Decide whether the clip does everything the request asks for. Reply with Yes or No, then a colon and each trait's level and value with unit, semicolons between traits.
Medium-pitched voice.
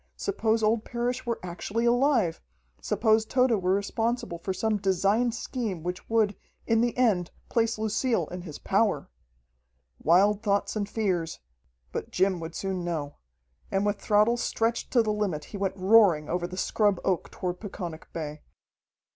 No: high, 205 Hz